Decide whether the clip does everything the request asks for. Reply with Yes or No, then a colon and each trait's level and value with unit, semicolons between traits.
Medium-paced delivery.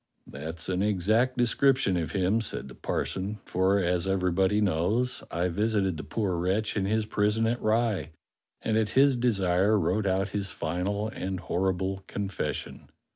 Yes: average, 160 wpm